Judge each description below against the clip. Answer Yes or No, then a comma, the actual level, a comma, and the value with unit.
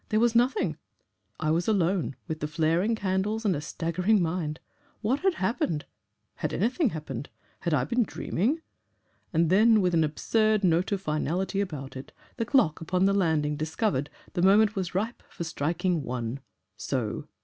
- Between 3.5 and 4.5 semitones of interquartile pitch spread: No, wide, 5.5 semitones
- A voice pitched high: No, medium, 180 Hz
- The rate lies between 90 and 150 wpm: No, average, 165 wpm